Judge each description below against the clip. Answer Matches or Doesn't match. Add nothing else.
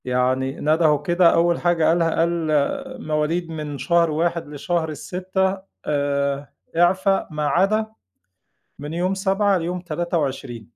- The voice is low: Doesn't match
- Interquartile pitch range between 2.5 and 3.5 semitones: Matches